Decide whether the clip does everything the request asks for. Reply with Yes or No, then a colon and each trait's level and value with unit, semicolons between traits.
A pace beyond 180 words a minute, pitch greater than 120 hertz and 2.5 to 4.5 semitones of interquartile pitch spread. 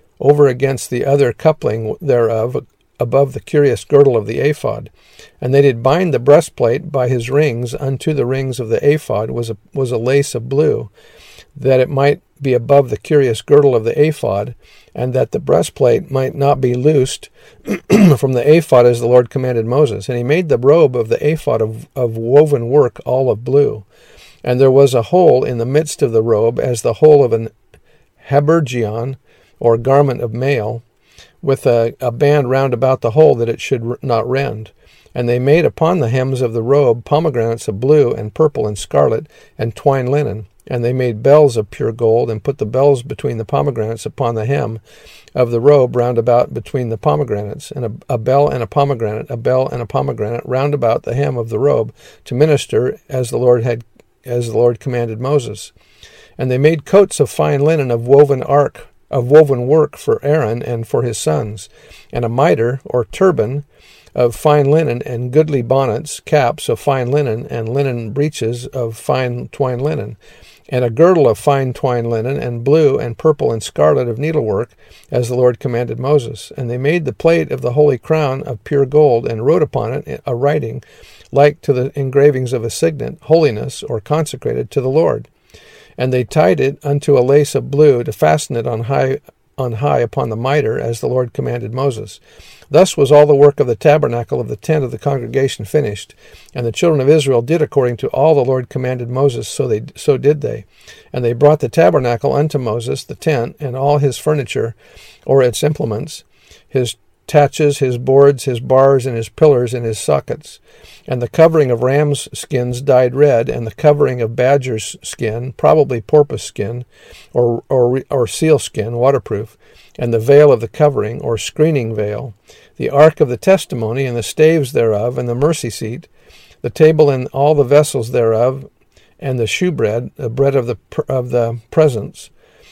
Yes: average, 190 wpm; low, 135 Hz; average, 3.6 semitones